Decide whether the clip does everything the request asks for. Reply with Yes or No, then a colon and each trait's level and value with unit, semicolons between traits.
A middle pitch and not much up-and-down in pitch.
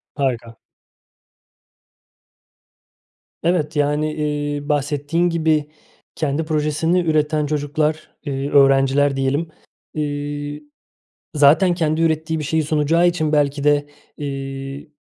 Yes: medium, 150 Hz; narrow, 1.5 semitones